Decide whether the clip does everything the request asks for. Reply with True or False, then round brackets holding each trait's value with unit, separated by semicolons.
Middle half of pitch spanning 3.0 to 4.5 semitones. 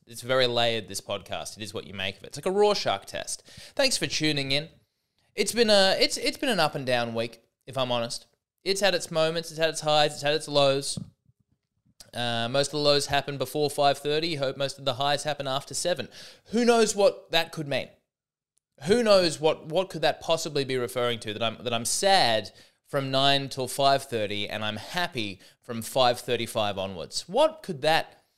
False (5.4 semitones)